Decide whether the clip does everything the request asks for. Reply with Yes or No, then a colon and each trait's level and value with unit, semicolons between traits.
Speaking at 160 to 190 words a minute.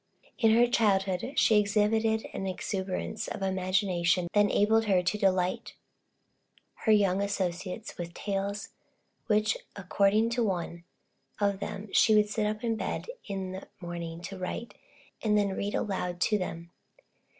No: average, 145 wpm